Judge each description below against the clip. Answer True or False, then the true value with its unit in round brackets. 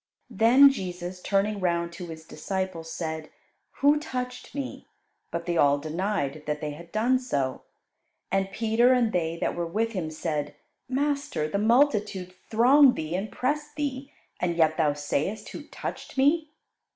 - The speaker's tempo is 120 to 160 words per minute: True (155 wpm)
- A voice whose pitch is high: True (195 Hz)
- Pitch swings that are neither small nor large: False (7.5 semitones)